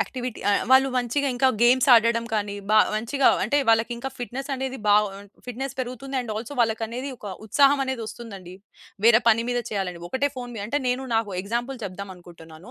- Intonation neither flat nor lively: Yes, average, 3.6 semitones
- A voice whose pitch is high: Yes, high, 235 Hz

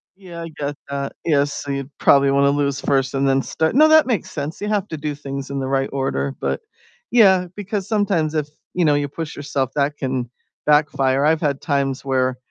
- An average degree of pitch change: Yes, average, 3.2 semitones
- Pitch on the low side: No, medium, 145 Hz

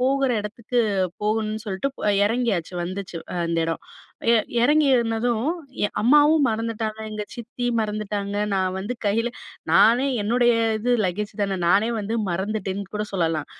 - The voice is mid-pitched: No, high, 215 Hz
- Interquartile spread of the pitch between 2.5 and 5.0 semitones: Yes, average, 3.3 semitones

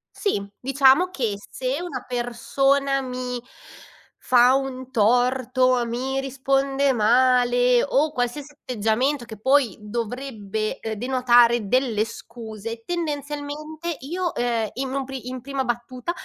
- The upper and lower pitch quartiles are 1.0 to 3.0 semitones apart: Yes, narrow, 2.4 semitones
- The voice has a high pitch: Yes, very high, 255 Hz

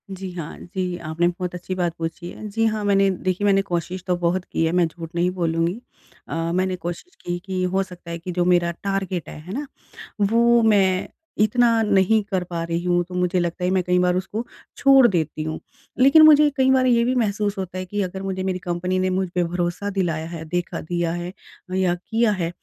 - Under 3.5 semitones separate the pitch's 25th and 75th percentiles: Yes, narrow, 2.4 semitones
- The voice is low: No, medium, 185 Hz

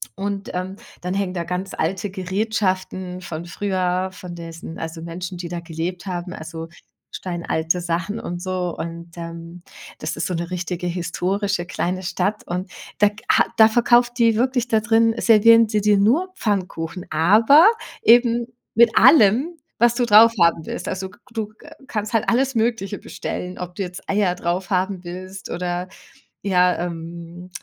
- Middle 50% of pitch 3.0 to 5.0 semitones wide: Yes, average, 3.6 semitones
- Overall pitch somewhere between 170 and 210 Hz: Yes, medium, 185 Hz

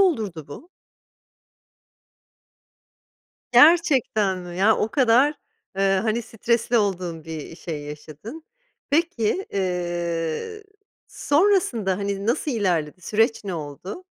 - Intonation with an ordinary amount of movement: No, wide, 6.1 semitones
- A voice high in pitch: Yes, high, 205 Hz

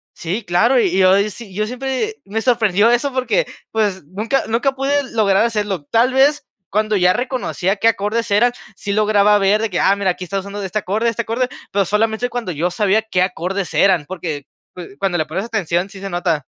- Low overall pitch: No, high, 205 Hz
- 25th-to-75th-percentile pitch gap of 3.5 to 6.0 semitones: Yes, average, 3.8 semitones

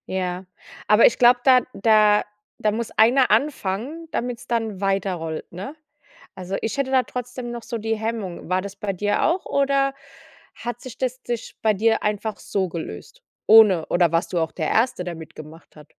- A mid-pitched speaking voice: No, high, 215 Hz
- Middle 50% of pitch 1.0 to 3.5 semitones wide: No, average, 4.5 semitones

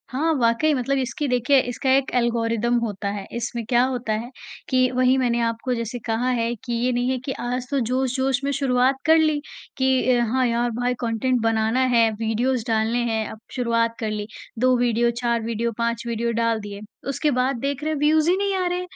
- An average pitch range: No, narrow, 2.2 semitones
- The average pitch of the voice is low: No, high, 245 Hz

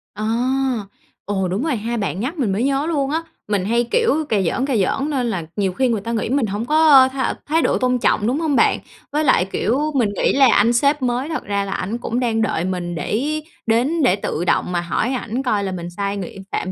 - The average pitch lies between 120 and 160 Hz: No, high, 235 Hz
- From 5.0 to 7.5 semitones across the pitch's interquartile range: Yes, average, 5.3 semitones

